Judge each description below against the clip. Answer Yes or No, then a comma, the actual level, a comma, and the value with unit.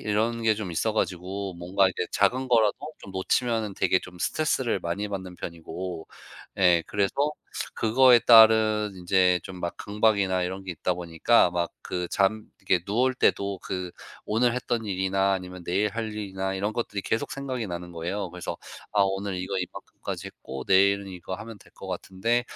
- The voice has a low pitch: Yes, very low, 95 Hz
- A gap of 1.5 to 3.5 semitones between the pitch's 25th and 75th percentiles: Yes, average, 3.2 semitones